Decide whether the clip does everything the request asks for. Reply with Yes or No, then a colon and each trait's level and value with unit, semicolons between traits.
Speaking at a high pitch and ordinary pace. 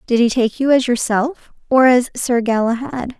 Yes: very high, 250 Hz; average, 190 wpm